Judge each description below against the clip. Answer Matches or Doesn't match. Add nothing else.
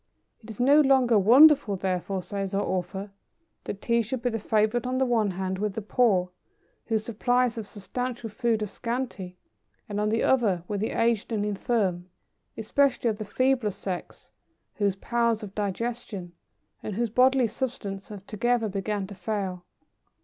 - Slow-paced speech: Doesn't match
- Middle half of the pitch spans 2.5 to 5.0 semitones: Matches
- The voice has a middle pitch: Doesn't match